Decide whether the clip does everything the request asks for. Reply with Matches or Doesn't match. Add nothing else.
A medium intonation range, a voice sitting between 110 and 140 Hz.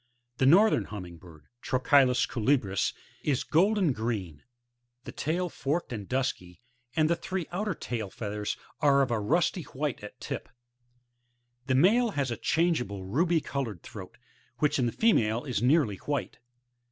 Doesn't match